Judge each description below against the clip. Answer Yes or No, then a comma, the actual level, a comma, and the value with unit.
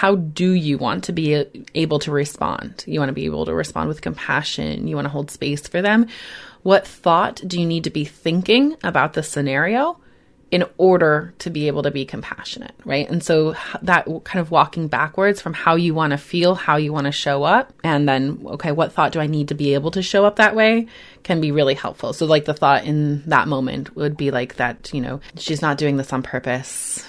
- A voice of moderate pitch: Yes, medium, 155 Hz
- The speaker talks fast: Yes, fast, 230 wpm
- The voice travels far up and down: No, average, 3.9 semitones